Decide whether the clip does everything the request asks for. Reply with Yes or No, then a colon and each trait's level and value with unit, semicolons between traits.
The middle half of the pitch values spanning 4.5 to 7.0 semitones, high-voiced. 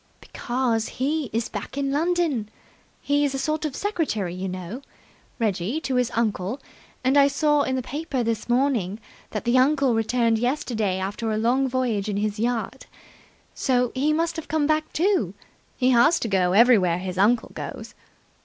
Yes: average, 4.8 semitones; high, 245 Hz